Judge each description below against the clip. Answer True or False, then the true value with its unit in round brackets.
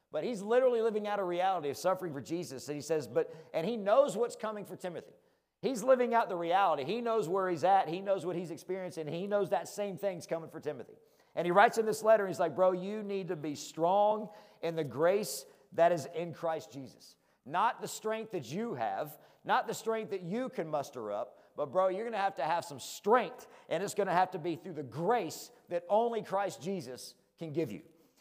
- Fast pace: True (230 wpm)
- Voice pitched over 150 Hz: True (185 Hz)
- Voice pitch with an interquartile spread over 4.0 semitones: True (4.7 semitones)